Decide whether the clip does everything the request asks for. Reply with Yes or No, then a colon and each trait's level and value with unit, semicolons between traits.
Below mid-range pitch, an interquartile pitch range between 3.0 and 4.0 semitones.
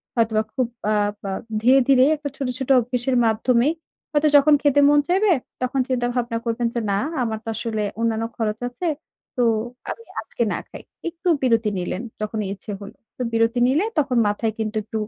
No: high, 240 Hz; average, 3.6 semitones